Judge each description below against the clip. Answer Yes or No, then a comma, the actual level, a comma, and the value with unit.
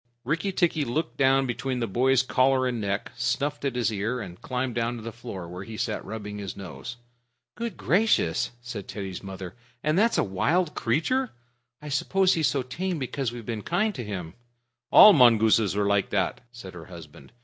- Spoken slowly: No, average, 190 wpm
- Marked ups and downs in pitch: Yes, wide, 5.9 semitones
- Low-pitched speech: Yes, low, 120 Hz